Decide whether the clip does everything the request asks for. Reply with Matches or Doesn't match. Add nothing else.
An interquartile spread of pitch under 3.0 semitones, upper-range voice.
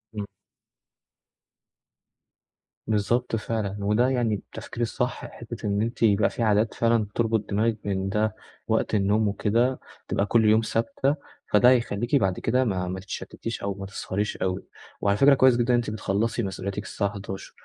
Doesn't match